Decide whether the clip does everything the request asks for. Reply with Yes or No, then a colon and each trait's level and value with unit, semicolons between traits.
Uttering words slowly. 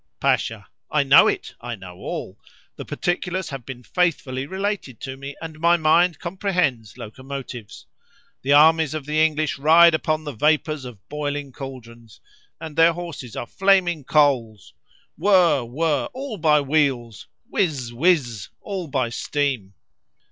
Yes: slow, 125 wpm